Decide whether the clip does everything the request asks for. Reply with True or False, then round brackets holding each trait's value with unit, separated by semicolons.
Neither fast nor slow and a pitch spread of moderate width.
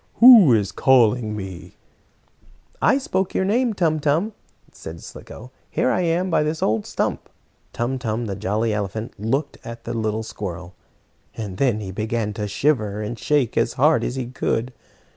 False (165 wpm; 6.0 semitones)